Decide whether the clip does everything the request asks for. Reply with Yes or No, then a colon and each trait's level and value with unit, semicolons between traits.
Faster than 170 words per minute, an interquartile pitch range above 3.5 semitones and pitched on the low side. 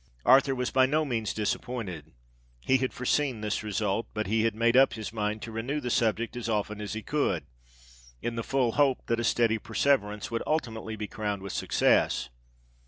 No: average, 185 wpm; average, 3.2 semitones; low, 115 Hz